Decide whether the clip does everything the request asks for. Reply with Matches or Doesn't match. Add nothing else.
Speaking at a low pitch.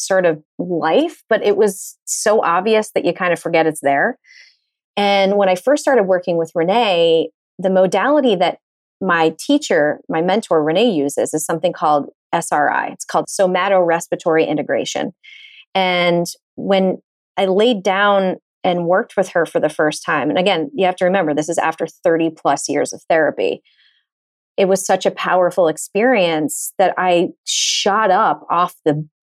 Doesn't match